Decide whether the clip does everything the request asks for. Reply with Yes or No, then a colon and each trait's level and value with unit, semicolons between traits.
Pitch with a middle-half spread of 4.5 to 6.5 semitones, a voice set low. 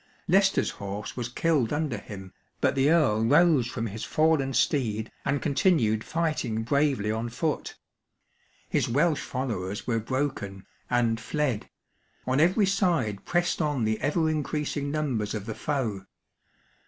Yes: wide, 5.6 semitones; low, 130 Hz